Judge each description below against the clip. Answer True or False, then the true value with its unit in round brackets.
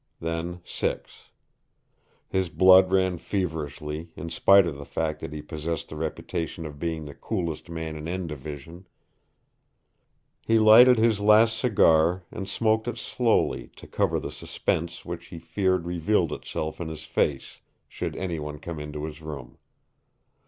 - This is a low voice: True (85 Hz)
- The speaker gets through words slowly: False (150 wpm)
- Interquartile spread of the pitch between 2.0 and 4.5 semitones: True (3.5 semitones)